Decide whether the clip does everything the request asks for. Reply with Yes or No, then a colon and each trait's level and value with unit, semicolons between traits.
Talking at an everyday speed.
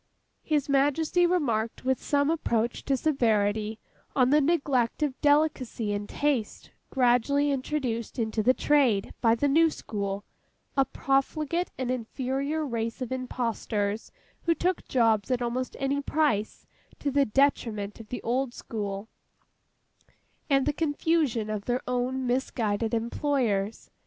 No: slow, 130 wpm